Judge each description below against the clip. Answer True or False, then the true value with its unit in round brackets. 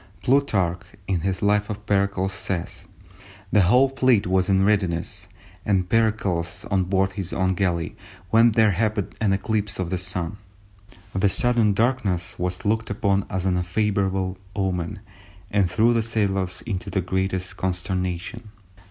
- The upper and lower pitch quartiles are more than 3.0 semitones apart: False (2.4 semitones)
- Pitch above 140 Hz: False (95 Hz)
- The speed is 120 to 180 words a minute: True (145 wpm)